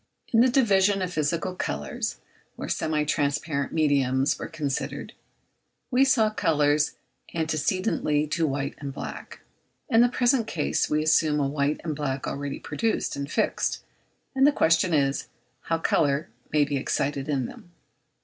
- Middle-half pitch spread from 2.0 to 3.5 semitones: No, average, 4.6 semitones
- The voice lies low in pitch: No, medium, 155 Hz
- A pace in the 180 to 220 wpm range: No, average, 150 wpm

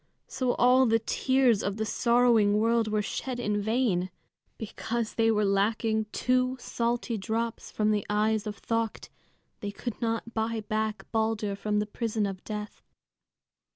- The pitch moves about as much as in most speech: No, narrow, 1.9 semitones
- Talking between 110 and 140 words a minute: No, average, 155 wpm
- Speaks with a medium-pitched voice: No, high, 220 Hz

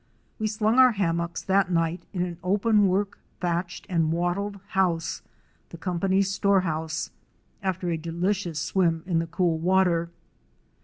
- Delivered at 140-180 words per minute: Yes, average, 145 wpm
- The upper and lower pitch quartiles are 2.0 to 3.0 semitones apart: Yes, average, 2.7 semitones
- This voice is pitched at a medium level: Yes, medium, 180 Hz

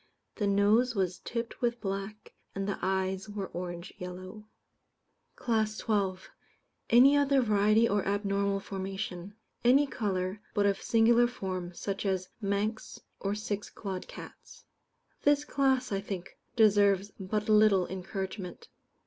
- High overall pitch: Yes, high, 200 Hz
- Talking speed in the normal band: No, slow, 130 wpm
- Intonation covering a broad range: No, narrow, 2.4 semitones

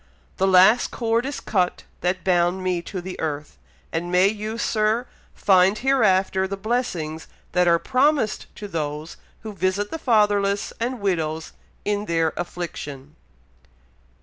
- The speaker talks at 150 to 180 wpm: No, average, 140 wpm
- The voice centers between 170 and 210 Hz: Yes, high, 190 Hz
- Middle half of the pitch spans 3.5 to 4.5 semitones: Yes, average, 3.8 semitones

